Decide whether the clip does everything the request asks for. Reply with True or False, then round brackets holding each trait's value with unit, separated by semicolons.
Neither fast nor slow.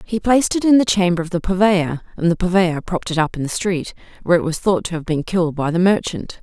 False (270 wpm)